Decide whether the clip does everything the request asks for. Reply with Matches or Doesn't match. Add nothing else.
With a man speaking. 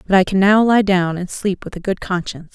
Doesn't match